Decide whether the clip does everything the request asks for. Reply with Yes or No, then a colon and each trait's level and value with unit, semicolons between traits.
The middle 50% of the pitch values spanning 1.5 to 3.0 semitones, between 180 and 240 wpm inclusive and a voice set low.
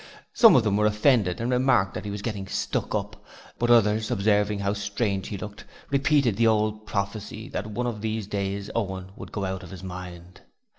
Yes: narrow, 2.4 semitones; average, 200 wpm; low, 105 Hz